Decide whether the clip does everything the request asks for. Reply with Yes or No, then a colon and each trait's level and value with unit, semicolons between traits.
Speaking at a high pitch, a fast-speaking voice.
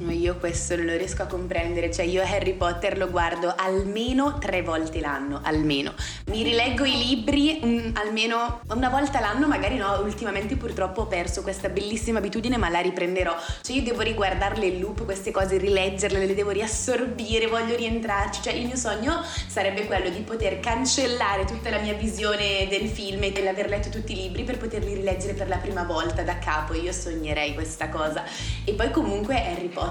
Yes: high, 200 Hz; fast, 185 wpm